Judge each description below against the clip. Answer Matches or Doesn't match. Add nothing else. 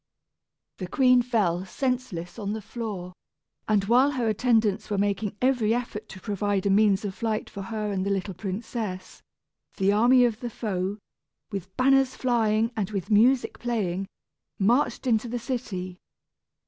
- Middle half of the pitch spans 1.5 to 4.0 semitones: Matches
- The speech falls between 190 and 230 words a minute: Doesn't match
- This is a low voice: Doesn't match